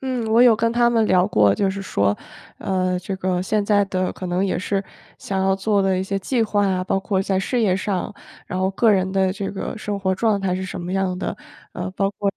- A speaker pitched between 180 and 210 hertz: Yes, high, 195 Hz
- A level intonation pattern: Yes, narrow, 1.8 semitones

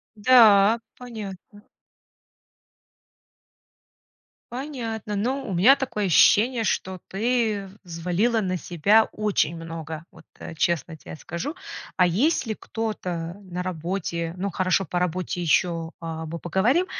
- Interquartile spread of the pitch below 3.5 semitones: No, average, 4.7 semitones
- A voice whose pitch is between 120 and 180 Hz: No, high, 190 Hz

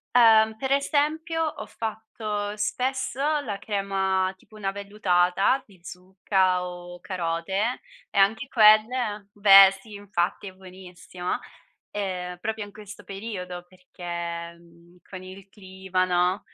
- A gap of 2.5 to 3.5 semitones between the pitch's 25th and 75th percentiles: Yes, average, 2.9 semitones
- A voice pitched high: Yes, high, 195 Hz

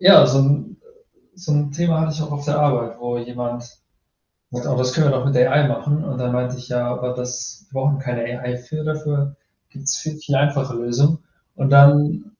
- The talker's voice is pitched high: No, medium, 140 Hz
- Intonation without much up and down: No, average, 3.1 semitones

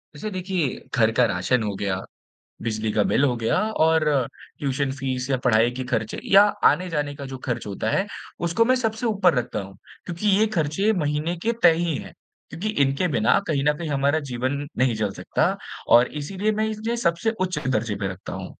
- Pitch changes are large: Yes, wide, 7.3 semitones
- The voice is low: No, medium, 145 Hz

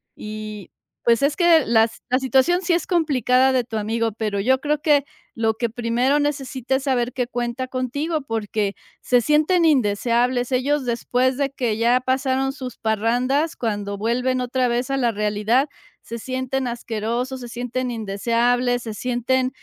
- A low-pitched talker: No, very high, 250 Hz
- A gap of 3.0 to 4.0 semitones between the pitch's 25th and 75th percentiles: No, narrow, 2.5 semitones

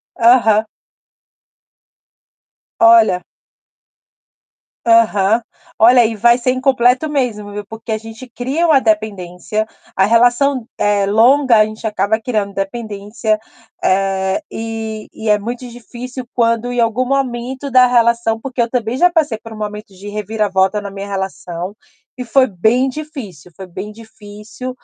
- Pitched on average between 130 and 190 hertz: No, high, 225 Hz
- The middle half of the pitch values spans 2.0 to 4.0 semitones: Yes, average, 3.1 semitones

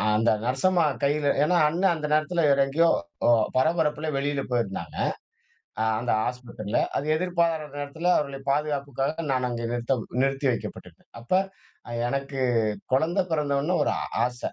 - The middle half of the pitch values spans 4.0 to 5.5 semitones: No, average, 3.6 semitones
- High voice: No, medium, 140 Hz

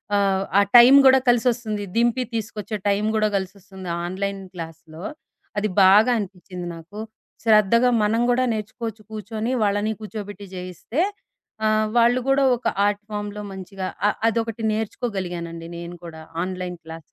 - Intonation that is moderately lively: Yes, average, 3.1 semitones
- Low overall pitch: No, high, 205 Hz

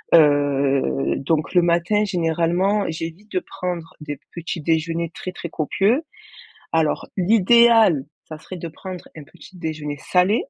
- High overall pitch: No, medium, 170 Hz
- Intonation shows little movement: No, average, 3.2 semitones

